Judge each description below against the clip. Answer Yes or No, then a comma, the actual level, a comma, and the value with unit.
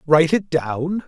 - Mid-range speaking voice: Yes, medium, 160 Hz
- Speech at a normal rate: Yes, average, 165 wpm